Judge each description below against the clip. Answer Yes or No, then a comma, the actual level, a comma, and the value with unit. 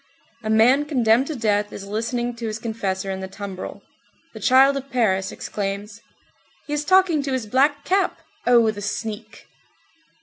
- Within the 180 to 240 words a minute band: No, average, 165 wpm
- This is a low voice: No, high, 230 Hz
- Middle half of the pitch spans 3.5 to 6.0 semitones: Yes, average, 4.8 semitones